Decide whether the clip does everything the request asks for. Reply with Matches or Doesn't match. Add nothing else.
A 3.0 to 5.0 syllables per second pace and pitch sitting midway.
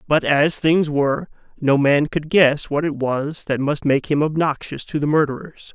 Matches